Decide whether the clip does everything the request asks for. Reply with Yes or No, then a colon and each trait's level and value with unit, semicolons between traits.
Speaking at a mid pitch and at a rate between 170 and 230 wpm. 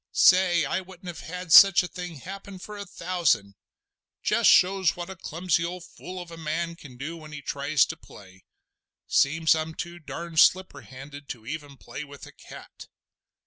Yes: medium, 170 Hz; average, 175 wpm